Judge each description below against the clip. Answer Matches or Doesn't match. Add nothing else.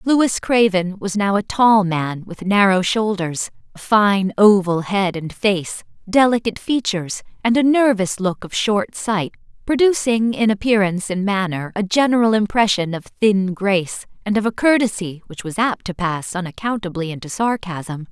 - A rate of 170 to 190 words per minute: Doesn't match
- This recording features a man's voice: Doesn't match